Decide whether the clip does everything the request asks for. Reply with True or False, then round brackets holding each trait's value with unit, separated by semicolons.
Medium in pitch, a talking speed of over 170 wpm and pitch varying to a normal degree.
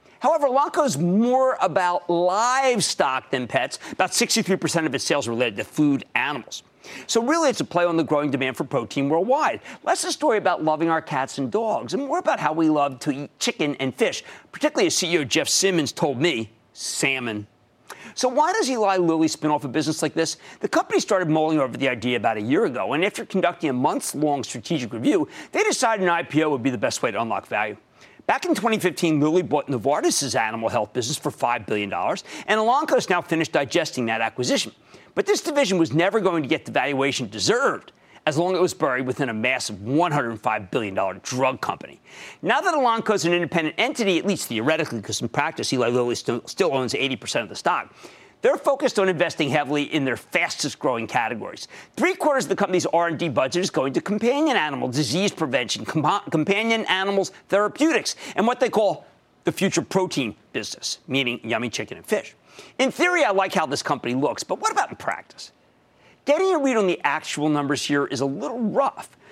False (165 Hz; 200 wpm; 7.8 semitones)